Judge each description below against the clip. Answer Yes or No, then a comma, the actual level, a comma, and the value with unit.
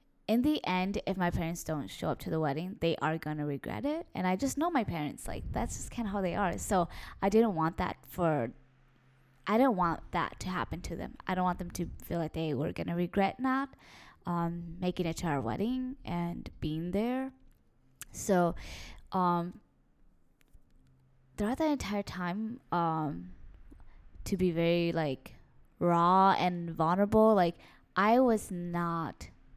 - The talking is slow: No, average, 170 wpm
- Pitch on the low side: No, medium, 175 Hz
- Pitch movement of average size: Yes, average, 4.3 semitones